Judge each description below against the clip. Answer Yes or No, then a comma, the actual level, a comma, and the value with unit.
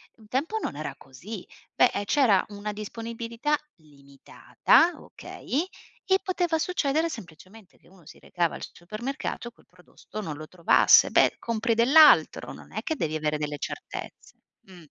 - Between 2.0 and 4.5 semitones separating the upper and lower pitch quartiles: No, wide, 8.4 semitones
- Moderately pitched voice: No, high, 215 Hz